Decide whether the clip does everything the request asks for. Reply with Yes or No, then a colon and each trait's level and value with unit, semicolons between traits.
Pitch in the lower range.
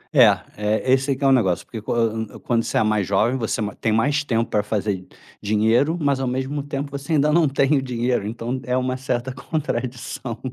Yes: low, 125 Hz